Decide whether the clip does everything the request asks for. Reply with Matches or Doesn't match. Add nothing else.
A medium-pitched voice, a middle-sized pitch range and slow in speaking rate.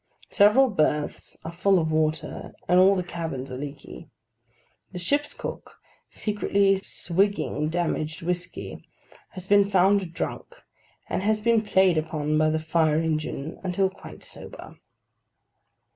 Matches